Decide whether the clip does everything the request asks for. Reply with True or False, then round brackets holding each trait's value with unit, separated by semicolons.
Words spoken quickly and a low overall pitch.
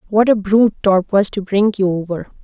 False (220 wpm; 200 Hz)